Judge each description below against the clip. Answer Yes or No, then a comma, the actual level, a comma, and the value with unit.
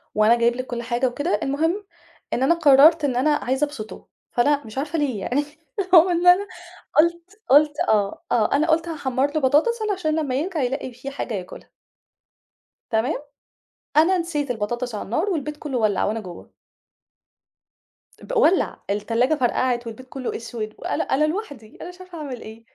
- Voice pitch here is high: Yes, very high, 275 Hz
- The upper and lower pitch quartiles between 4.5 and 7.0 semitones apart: Yes, average, 5.0 semitones